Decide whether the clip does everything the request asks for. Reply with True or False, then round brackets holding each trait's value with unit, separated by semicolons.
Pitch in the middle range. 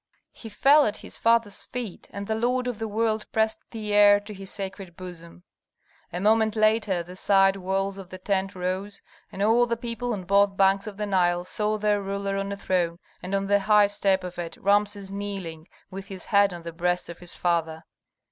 False (200 Hz)